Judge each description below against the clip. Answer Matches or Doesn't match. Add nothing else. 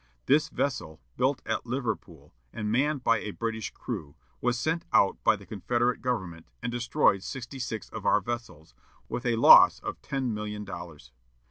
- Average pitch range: Matches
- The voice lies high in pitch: Doesn't match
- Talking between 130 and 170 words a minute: Matches